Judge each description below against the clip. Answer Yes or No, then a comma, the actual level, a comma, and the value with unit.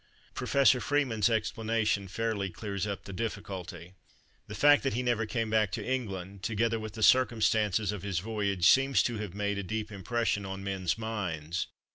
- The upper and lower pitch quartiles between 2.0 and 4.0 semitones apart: Yes, average, 2.7 semitones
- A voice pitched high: No, low, 105 Hz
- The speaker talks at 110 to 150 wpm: No, average, 165 wpm